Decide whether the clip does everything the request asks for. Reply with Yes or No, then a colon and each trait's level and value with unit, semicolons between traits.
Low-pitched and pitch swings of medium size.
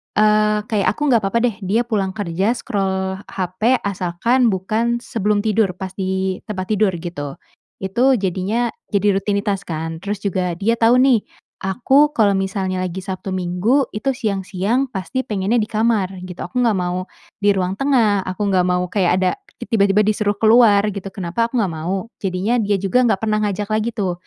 No: high, 200 Hz; average, 3.0 semitones